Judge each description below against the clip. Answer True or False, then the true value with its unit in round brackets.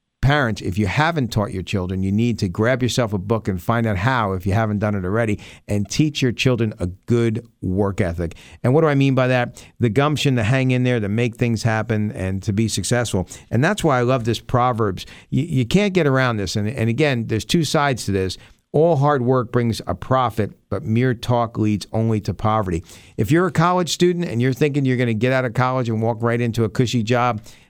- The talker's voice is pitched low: True (115 Hz)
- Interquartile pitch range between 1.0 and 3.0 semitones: False (3.7 semitones)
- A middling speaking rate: False (235 wpm)